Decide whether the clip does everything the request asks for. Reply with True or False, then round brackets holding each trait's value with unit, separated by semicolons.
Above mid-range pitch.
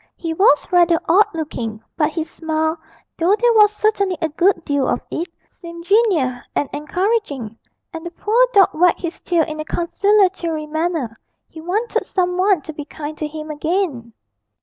True (335 Hz)